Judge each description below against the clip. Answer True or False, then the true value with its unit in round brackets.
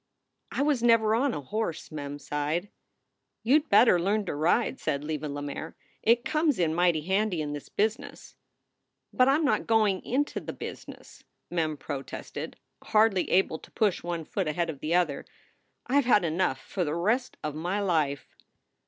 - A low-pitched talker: False (180 Hz)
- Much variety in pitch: True (6.6 semitones)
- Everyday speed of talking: True (175 wpm)